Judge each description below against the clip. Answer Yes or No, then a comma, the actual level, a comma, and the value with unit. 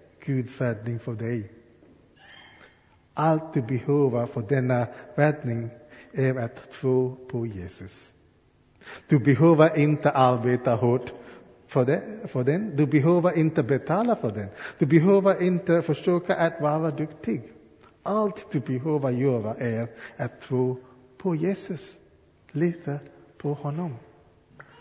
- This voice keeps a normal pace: No, slow, 115 wpm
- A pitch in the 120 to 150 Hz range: Yes, low, 135 Hz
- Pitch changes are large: No, average, 4.8 semitones